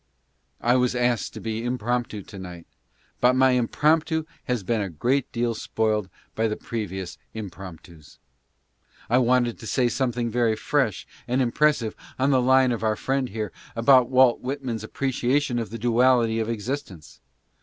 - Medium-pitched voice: No, low, 120 Hz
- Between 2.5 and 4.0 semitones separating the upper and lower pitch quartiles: Yes, average, 2.8 semitones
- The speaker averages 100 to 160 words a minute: Yes, average, 155 wpm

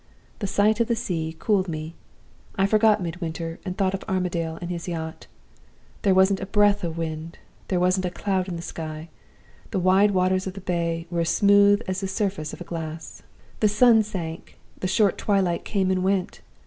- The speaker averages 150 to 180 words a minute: No, average, 195 wpm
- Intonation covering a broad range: No, average, 3.1 semitones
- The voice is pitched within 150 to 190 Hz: Yes, medium, 185 Hz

